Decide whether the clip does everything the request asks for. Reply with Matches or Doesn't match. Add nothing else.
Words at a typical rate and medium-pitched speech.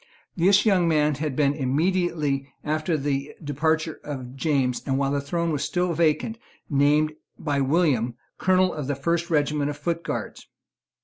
Matches